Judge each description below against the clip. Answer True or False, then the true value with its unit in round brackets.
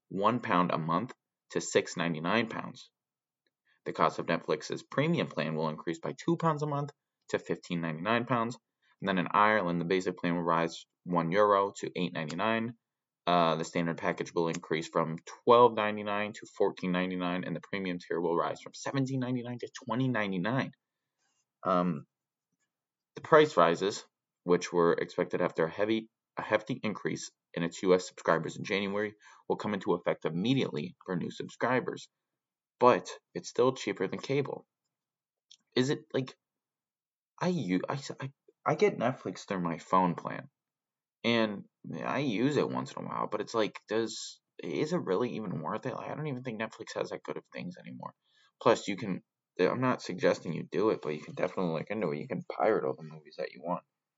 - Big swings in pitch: True (6.0 semitones)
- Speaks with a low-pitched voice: True (100 Hz)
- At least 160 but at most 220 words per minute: True (175 wpm)